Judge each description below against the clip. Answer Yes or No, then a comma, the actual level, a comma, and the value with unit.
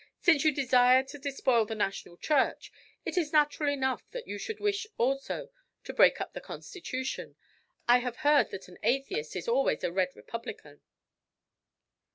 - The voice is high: Yes, very high, 265 Hz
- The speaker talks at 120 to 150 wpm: No, average, 165 wpm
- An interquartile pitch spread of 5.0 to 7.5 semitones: No, average, 4.3 semitones